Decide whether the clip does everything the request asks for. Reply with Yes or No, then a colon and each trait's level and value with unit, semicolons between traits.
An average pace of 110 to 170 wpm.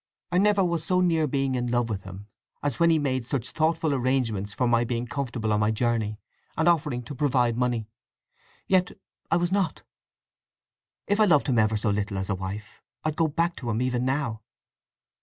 No: average, 195 wpm